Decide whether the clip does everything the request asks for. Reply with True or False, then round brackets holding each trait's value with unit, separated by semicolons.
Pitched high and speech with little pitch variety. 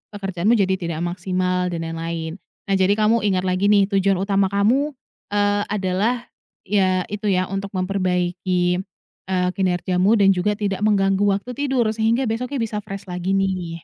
True (195 Hz; 2.2 semitones)